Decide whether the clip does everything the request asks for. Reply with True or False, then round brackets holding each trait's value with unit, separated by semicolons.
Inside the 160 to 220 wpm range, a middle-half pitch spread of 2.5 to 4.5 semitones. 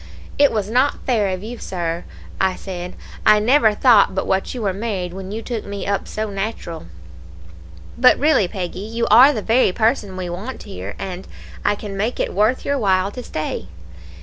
True (190 wpm; 3.7 semitones)